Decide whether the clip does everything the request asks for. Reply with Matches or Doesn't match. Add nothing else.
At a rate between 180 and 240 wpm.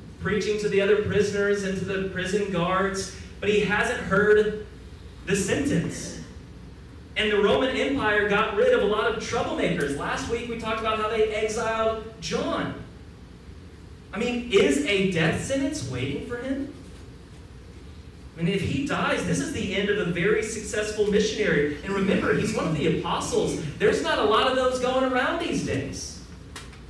Doesn't match